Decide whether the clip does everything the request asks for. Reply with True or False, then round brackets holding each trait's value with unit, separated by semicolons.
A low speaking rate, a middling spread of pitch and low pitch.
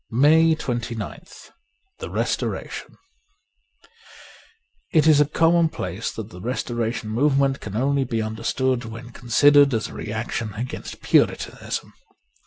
True (125 wpm; 4.3 semitones; 125 Hz)